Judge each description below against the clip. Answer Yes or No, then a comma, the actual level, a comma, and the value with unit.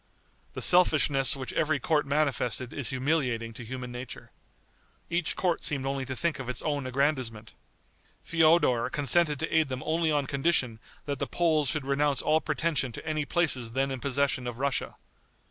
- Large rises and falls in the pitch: No, average, 3.3 semitones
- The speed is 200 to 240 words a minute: No, average, 170 wpm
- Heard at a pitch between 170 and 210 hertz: No, medium, 140 Hz